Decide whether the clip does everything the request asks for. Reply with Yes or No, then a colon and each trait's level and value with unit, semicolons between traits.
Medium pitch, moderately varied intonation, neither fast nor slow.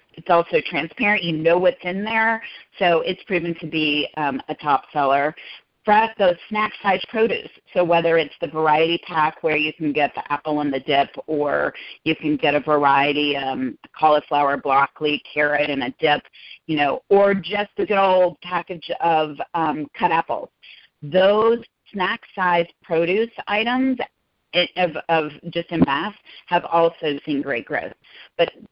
Yes: medium, 165 Hz; average, 4.2 semitones; average, 160 wpm